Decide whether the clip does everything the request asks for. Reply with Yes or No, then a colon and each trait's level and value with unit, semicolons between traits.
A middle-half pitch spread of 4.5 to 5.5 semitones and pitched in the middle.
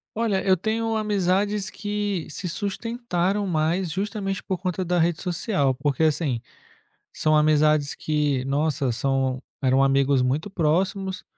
Yes: average, 5.2 semitones; medium, 175 Hz